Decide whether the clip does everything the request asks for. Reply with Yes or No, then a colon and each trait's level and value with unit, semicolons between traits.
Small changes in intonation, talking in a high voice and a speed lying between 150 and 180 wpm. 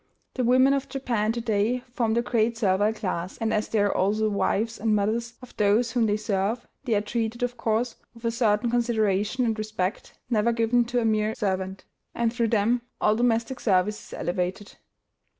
No: narrow, 2.3 semitones; high, 225 Hz; average, 195 wpm